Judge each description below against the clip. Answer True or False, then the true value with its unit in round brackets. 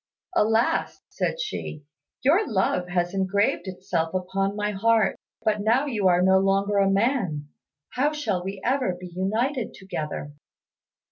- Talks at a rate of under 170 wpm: True (140 wpm)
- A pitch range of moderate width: True (3.6 semitones)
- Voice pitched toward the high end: True (195 Hz)